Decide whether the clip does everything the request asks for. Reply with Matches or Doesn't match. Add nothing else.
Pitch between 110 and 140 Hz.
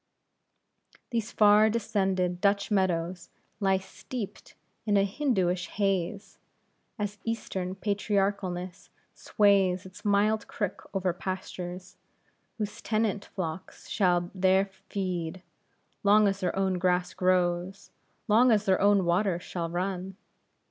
Doesn't match